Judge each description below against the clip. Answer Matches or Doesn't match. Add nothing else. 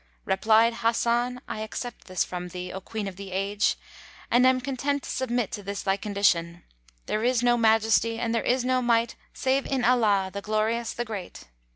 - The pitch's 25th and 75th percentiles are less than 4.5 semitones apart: Matches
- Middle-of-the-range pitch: Doesn't match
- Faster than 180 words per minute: Matches